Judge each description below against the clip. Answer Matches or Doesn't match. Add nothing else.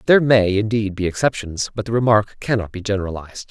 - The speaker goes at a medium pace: Matches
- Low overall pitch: Matches